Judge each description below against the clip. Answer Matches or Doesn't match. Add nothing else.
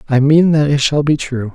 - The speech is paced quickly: Matches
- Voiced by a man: Matches